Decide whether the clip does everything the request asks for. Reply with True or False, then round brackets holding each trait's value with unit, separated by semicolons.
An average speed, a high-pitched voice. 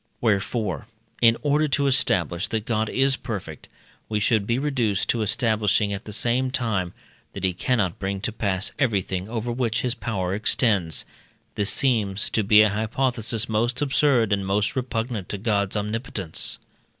False (160 wpm; 110 Hz)